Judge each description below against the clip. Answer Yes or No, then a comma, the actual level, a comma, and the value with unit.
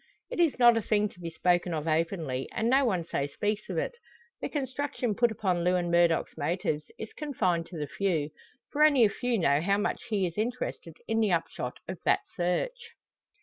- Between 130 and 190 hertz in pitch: Yes, medium, 185 Hz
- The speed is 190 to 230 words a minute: Yes, average, 200 wpm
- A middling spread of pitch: No, wide, 5.8 semitones